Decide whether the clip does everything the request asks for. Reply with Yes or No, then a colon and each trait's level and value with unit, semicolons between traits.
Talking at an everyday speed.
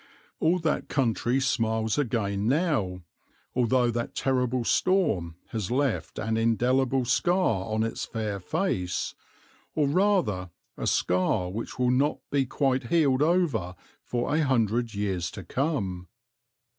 No: slow, 130 wpm